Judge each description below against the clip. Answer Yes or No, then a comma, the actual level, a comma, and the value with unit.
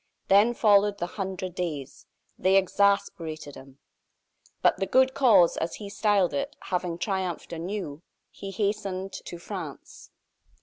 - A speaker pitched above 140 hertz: Yes, high, 190 Hz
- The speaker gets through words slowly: Yes, slow, 130 wpm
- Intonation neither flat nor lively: Yes, average, 3.0 semitones